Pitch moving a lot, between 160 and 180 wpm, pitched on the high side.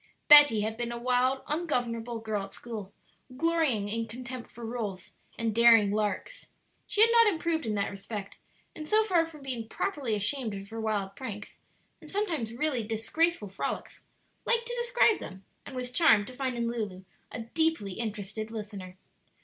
Yes: wide, 6.2 semitones; average, 170 wpm; high, 235 Hz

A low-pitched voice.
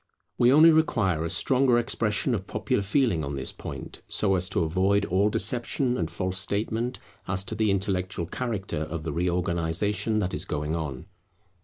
Yes: very low, 95 Hz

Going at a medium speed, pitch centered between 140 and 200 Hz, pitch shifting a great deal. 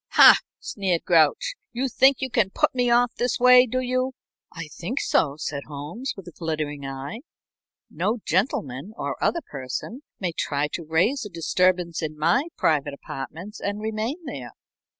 Yes: average, 165 wpm; medium, 185 Hz; wide, 8.2 semitones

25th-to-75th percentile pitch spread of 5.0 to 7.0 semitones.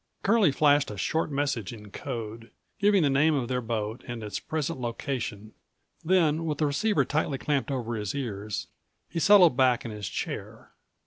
Yes: average, 5.3 semitones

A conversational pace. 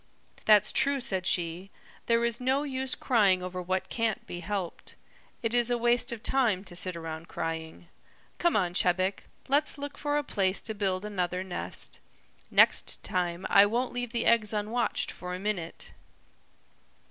Yes: average, 165 wpm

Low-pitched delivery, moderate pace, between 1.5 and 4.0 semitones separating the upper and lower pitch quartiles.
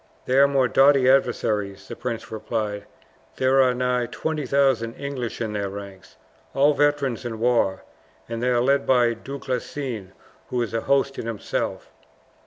Yes: low, 125 Hz; average, 160 wpm; average, 3.3 semitones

